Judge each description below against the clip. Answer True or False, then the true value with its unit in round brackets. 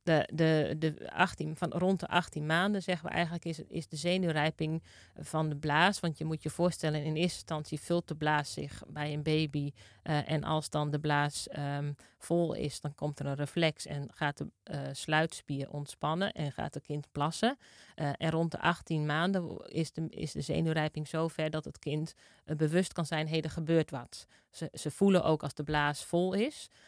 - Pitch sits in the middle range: True (155 Hz)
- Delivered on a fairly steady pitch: True (2.1 semitones)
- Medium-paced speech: False (205 wpm)